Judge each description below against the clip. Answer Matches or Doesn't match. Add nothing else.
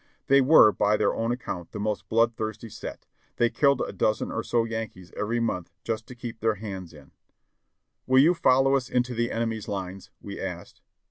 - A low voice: Matches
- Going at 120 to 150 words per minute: Doesn't match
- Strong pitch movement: Doesn't match